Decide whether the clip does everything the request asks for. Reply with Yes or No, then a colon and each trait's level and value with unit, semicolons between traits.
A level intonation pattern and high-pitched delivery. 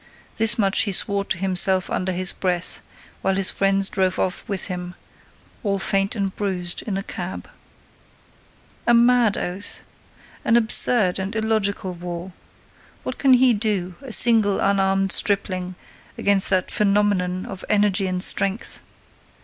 Yes: narrow, 2.0 semitones; high, 195 Hz